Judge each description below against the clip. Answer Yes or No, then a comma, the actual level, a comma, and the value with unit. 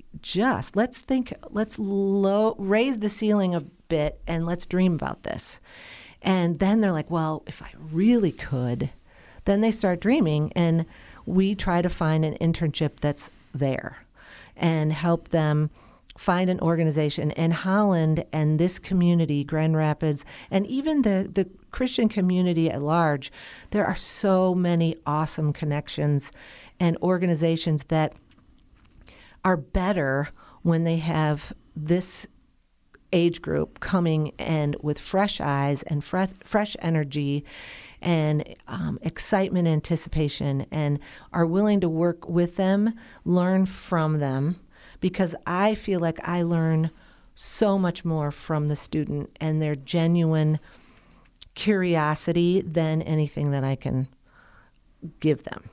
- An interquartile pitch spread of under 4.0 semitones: Yes, average, 3.6 semitones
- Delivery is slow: Yes, slow, 130 wpm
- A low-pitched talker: No, medium, 165 Hz